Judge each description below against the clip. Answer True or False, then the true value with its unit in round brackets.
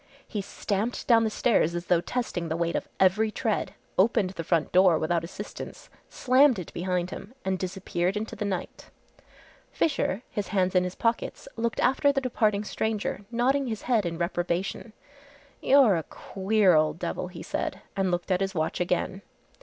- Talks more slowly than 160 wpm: False (175 wpm)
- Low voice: False (195 Hz)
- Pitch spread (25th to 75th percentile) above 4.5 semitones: False (4.0 semitones)